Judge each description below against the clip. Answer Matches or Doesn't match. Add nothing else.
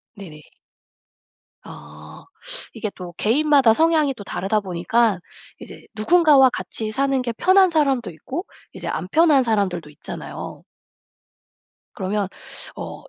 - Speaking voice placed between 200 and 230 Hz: Matches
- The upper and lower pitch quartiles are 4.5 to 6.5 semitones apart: Doesn't match